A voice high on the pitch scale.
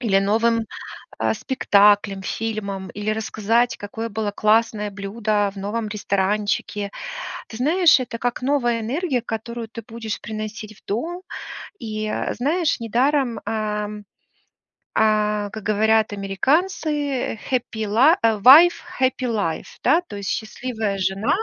Yes: high, 220 Hz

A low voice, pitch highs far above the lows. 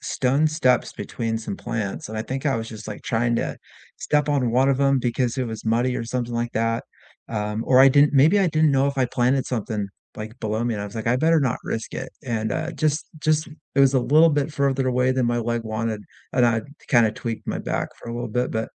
No: low, 125 Hz; average, 3.3 semitones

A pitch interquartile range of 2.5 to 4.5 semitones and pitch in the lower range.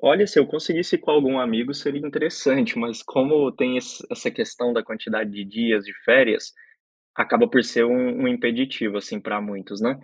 No: wide, 5.4 semitones; low, 125 Hz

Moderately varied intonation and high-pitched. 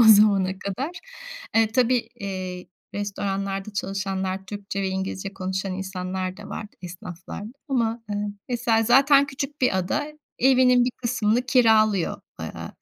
Yes: average, 4.1 semitones; high, 205 Hz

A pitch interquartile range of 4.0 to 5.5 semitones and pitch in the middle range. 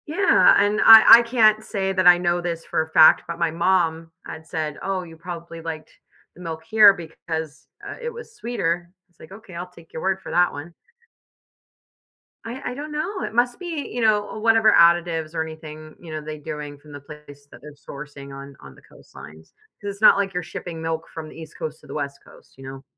Yes: average, 4.8 semitones; medium, 170 Hz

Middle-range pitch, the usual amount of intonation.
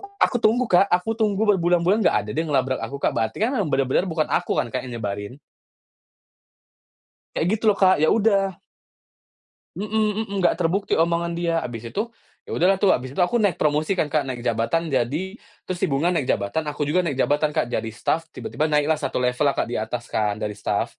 No: medium, 155 Hz; wide, 6.1 semitones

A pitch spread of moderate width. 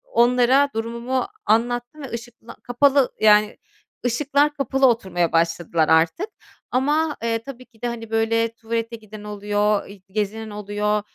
Yes: average, 3.1 semitones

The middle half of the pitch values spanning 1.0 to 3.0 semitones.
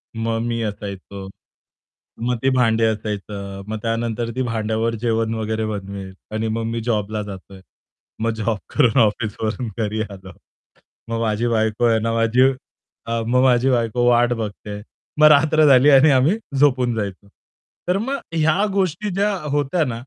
Yes: average, 2.7 semitones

